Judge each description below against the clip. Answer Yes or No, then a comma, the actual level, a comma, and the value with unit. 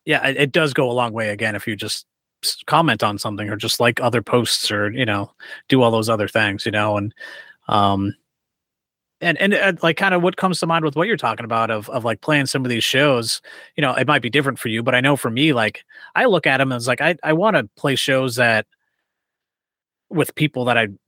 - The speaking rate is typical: No, fast, 240 wpm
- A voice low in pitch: Yes, low, 125 Hz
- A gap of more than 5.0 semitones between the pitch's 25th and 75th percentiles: Yes, wide, 5.5 semitones